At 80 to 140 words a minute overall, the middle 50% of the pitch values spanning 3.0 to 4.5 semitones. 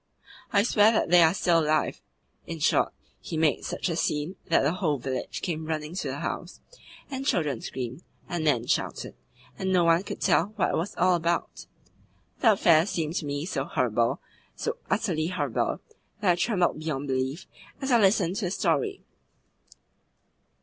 No: average, 175 wpm; average, 3.7 semitones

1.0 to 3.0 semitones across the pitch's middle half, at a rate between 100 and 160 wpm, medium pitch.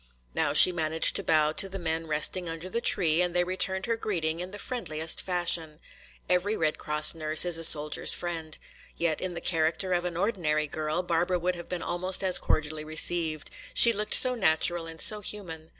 No: narrow, 2.6 semitones; average, 200 wpm; medium, 170 Hz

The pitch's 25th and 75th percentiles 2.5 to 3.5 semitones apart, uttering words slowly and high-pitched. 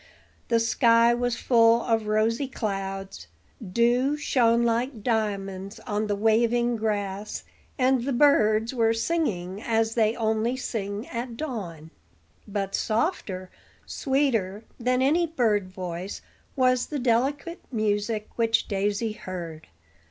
Yes: average, 3.1 semitones; slow, 120 wpm; high, 225 Hz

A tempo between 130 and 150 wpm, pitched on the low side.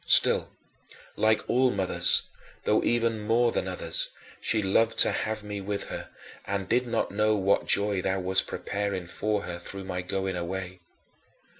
No: average, 160 wpm; low, 100 Hz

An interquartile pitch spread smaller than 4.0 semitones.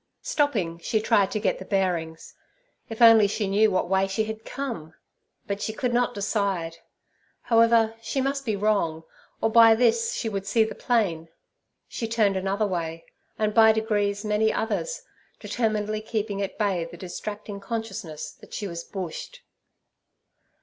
Yes: average, 2.8 semitones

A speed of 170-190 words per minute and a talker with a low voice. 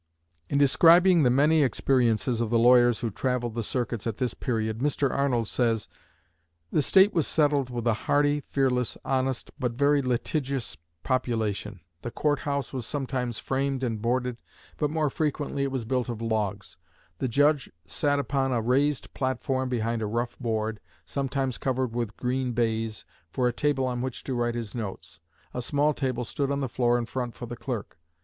Yes: average, 180 wpm; low, 125 Hz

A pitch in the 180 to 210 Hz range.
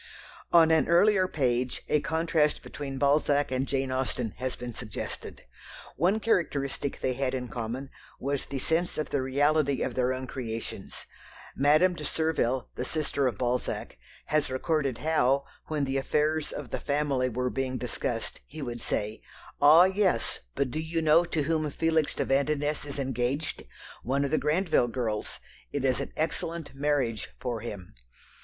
No: medium, 140 Hz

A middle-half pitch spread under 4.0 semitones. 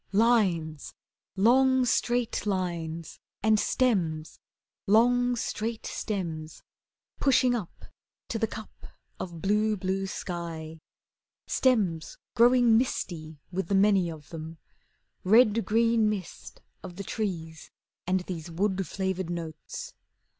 No: average, 5.3 semitones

